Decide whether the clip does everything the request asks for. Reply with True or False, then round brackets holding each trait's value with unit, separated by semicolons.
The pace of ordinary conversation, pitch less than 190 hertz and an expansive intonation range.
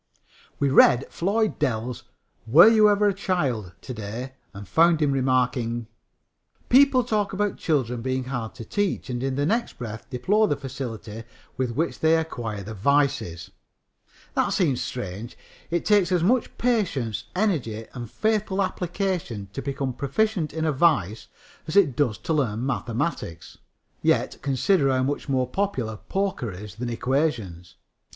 True (150 wpm; 135 Hz; 7.3 semitones)